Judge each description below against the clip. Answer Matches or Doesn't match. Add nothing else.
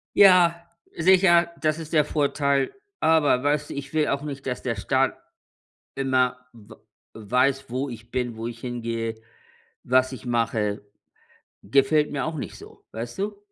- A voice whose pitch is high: Doesn't match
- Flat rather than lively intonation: Doesn't match